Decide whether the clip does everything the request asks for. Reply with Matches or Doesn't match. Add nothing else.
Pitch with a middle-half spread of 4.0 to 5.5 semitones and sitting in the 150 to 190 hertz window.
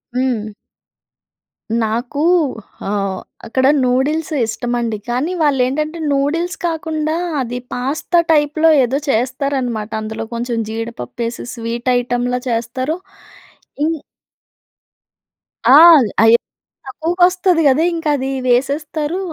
Doesn't match